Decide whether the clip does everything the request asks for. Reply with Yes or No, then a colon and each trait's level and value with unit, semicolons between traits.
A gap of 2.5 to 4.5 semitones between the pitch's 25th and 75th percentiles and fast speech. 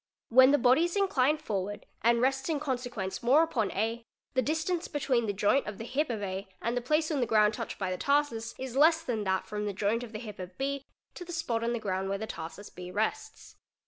No: wide, 5.5 semitones; fast, 250 wpm